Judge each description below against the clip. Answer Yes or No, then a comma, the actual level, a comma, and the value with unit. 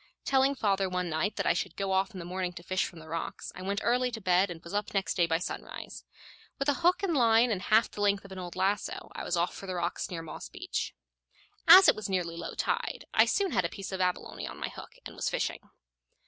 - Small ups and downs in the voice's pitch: No, average, 3.7 semitones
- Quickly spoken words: Yes, fast, 260 wpm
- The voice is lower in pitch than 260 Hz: Yes, high, 190 Hz